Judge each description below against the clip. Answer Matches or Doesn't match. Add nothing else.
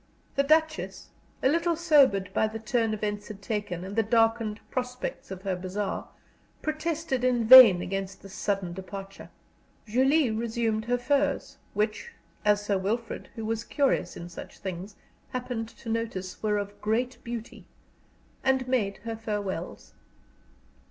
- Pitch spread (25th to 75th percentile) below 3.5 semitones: Doesn't match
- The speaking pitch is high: Matches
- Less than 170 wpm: Matches